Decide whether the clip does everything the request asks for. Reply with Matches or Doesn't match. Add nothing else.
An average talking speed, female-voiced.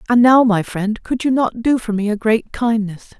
Doesn't match